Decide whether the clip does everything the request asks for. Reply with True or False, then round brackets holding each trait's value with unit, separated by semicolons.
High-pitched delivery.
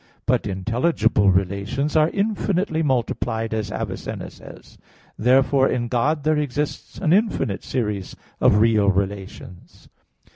False (120 Hz)